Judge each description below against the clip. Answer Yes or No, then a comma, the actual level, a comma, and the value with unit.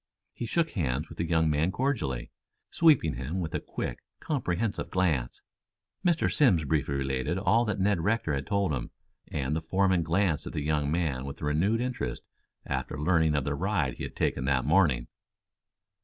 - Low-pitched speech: Yes, very low, 80 Hz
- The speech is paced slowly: No, average, 175 wpm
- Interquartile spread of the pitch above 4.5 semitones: Yes, wide, 5.5 semitones